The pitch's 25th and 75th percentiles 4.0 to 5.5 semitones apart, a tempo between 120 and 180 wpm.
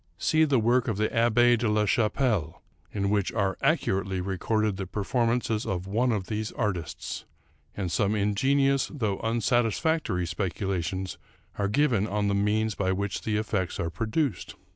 No: average, 3.3 semitones; average, 160 wpm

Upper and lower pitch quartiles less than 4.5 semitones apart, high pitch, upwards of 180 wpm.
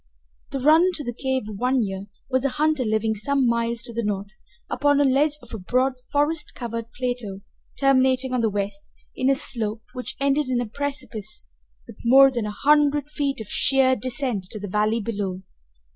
Yes: average, 4.1 semitones; very high, 250 Hz; average, 190 wpm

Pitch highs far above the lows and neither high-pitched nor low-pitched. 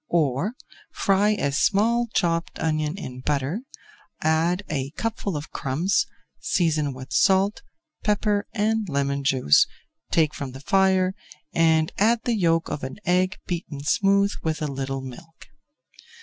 Yes: wide, 5.9 semitones; medium, 165 Hz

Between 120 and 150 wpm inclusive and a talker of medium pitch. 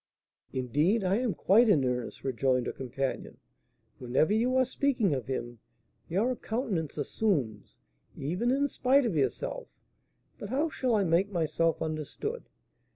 Yes: average, 140 wpm; medium, 180 Hz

